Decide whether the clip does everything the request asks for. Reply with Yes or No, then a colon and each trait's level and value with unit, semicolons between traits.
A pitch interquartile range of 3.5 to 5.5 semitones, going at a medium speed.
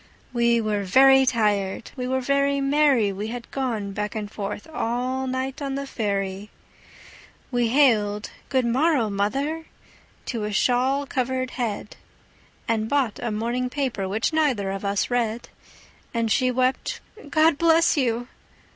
Yes: average, 4.1 semitones; average, 145 wpm